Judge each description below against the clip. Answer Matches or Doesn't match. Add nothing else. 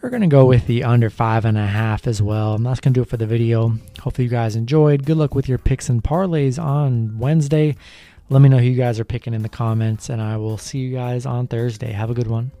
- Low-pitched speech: Matches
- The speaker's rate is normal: Doesn't match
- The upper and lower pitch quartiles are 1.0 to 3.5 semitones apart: Matches